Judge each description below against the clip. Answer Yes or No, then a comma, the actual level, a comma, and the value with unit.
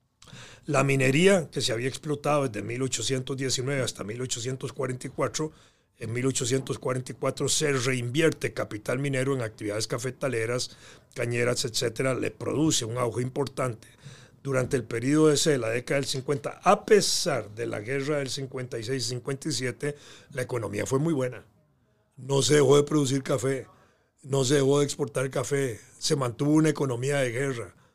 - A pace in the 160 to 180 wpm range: No, average, 135 wpm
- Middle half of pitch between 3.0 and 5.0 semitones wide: No, narrow, 2.4 semitones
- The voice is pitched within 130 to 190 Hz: Yes, low, 135 Hz